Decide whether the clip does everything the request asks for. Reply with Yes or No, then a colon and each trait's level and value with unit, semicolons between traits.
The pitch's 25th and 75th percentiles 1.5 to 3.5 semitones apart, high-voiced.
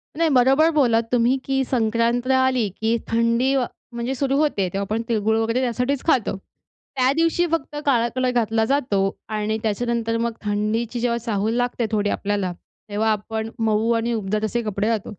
Yes: average, 2.8 semitones; high, 230 Hz